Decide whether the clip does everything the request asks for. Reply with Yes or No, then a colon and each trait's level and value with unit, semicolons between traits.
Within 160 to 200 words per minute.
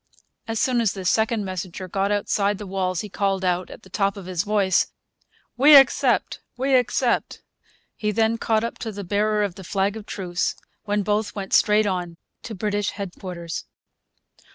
Yes: average, 175 wpm